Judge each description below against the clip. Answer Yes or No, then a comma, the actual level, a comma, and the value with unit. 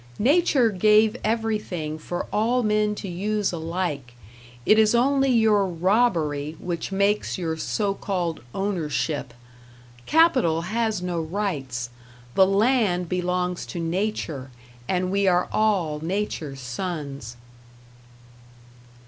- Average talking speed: No, slow, 110 wpm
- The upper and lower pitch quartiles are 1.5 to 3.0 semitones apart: No, average, 4.6 semitones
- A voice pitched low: No, medium, 185 Hz